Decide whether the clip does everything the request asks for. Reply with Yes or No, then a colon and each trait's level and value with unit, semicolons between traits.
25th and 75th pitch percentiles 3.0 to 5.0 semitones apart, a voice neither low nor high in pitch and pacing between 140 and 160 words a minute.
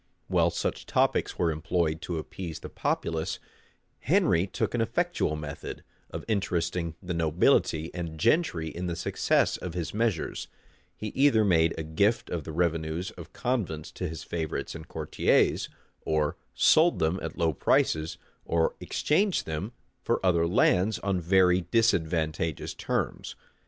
No: average, 3.4 semitones; very low, 85 Hz; average, 145 wpm